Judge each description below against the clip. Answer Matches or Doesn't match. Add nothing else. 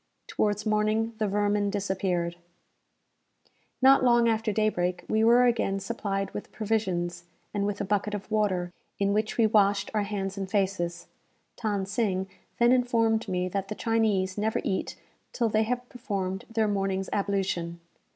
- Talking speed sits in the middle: Matches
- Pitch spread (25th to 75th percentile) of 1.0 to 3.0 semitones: Matches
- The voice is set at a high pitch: Matches